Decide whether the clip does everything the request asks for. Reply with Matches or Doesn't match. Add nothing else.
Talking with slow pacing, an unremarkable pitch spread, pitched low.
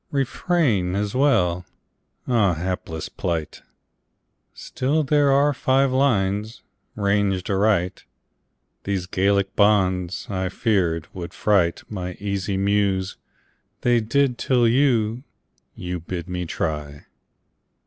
Matches